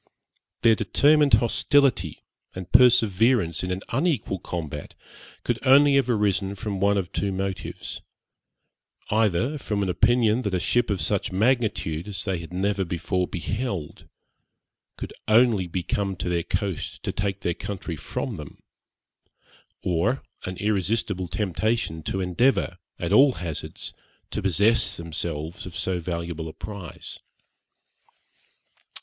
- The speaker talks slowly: Yes, slow, 130 wpm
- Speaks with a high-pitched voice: No, low, 100 Hz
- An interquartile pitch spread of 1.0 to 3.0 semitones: No, average, 4.3 semitones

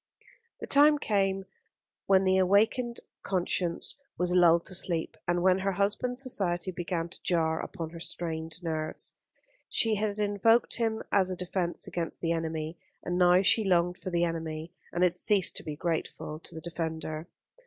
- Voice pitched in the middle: Yes, medium, 180 Hz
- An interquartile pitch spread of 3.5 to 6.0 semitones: No, average, 2.9 semitones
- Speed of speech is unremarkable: Yes, average, 165 wpm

